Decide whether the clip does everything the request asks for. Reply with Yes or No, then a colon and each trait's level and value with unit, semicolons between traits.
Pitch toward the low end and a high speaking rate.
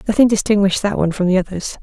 No: high, 195 Hz; fast, 230 wpm